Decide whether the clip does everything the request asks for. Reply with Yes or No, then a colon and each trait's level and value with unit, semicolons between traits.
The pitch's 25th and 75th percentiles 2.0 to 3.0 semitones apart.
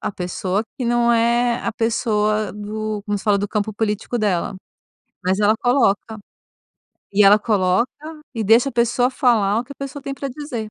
Yes: narrow, 2.6 semitones